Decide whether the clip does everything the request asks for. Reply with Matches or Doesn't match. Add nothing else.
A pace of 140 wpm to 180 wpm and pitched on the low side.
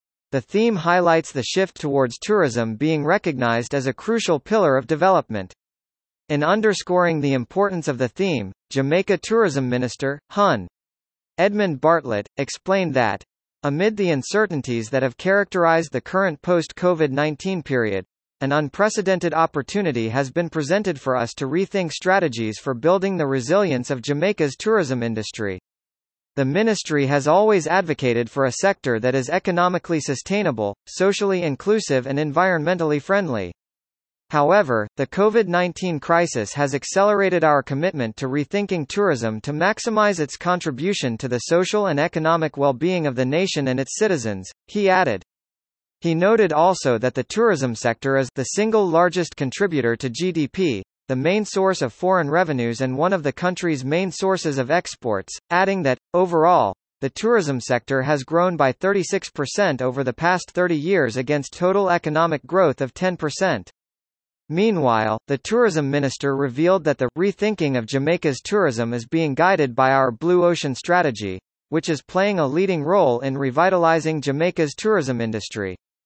Doesn't match